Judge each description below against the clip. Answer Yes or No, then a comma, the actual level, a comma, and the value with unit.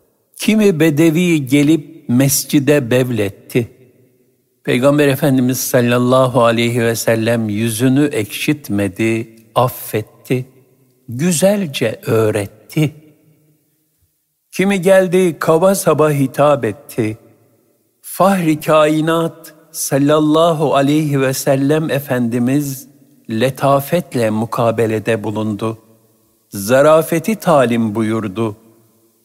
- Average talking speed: No, slow, 70 wpm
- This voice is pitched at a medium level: No, low, 130 Hz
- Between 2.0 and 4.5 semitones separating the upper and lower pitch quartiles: No, average, 5.1 semitones